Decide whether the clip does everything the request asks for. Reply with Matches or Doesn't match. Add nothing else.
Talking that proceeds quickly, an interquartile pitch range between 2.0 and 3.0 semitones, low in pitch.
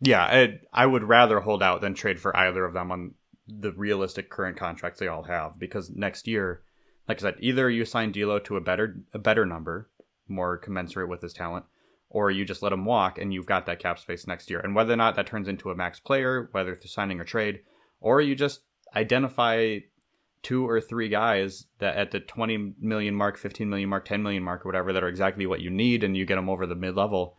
Doesn't match